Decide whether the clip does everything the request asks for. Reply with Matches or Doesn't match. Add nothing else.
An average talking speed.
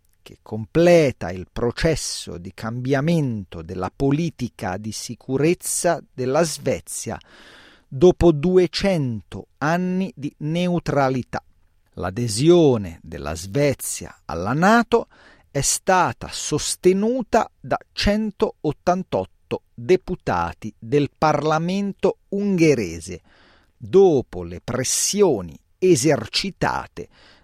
Doesn't match